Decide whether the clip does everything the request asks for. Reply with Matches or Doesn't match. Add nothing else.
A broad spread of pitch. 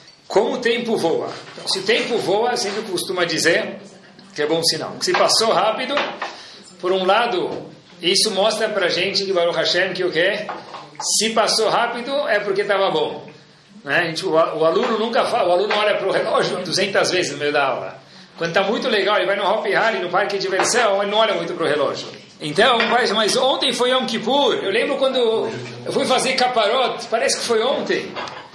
Doesn't match